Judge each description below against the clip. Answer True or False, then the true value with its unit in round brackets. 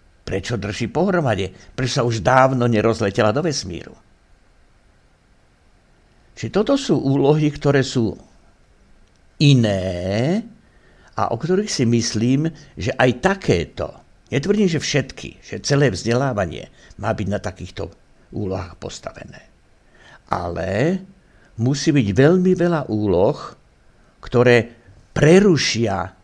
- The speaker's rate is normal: False (105 wpm)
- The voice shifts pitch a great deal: True (6.7 semitones)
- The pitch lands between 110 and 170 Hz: True (120 Hz)